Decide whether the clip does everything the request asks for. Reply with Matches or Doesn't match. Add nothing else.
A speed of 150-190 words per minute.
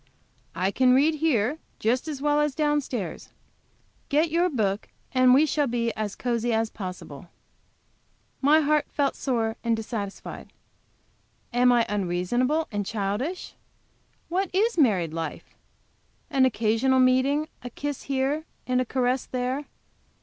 Doesn't match